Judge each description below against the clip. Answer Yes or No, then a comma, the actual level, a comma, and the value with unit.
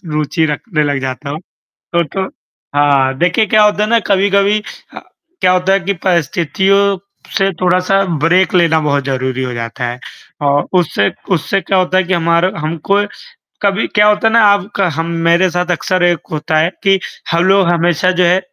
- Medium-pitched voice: Yes, medium, 175 Hz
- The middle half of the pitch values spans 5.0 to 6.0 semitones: No, average, 4.2 semitones